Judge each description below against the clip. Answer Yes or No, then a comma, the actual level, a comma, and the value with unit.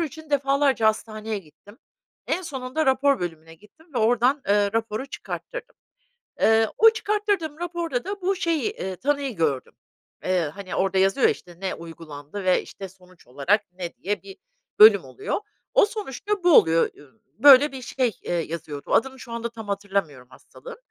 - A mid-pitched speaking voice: No, high, 225 Hz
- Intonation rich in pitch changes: Yes, wide, 8.4 semitones